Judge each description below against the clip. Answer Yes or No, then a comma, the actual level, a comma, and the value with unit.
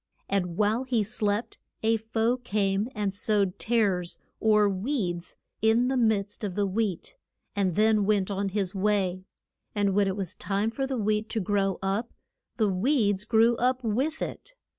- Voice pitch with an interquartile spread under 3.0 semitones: Yes, narrow, 2.6 semitones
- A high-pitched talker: Yes, high, 210 Hz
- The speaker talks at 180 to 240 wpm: No, average, 165 wpm